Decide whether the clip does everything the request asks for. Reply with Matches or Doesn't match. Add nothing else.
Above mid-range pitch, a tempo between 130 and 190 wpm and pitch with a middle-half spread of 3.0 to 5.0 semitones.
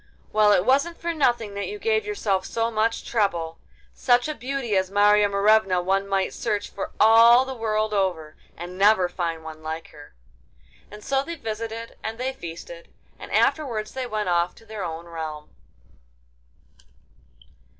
Matches